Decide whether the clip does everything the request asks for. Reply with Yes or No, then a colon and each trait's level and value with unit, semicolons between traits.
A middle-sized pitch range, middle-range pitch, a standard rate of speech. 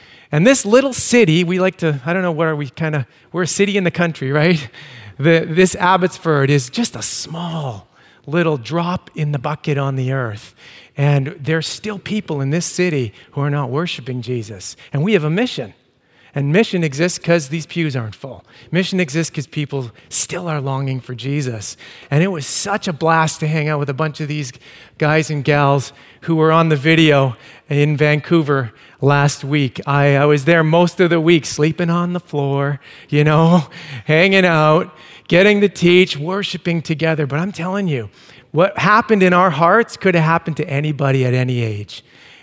Yes: average, 3.7 semitones; medium, 155 Hz; average, 190 wpm